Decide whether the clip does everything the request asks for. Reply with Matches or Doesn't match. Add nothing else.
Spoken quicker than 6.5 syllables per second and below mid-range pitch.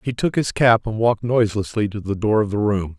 Doesn't match